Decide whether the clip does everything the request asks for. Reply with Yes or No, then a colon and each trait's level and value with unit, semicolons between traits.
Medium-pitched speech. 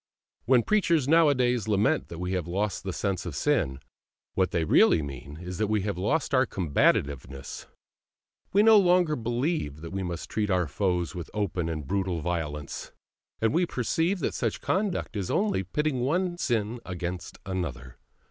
No: low, 100 Hz